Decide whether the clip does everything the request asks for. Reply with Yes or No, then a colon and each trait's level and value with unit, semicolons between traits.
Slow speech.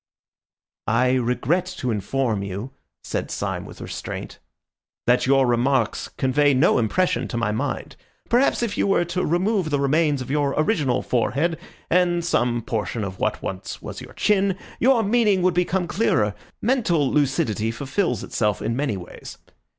No: average, 155 wpm